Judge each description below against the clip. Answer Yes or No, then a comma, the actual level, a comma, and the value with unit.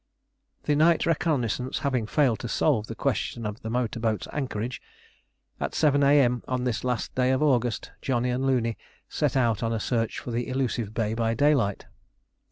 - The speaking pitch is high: No, low, 125 Hz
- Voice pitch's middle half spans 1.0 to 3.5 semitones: Yes, average, 2.9 semitones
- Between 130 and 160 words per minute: No, average, 175 wpm